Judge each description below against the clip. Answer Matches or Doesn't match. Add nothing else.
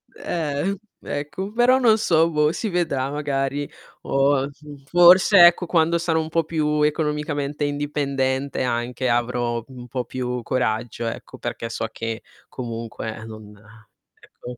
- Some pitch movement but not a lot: Matches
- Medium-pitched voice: Matches